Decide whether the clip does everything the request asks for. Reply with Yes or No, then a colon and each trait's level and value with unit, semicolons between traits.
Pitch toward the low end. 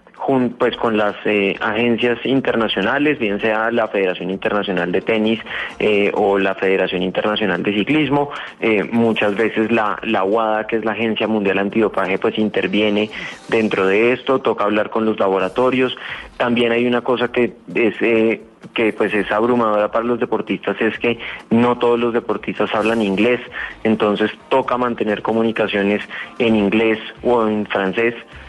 Yes: low, 110 Hz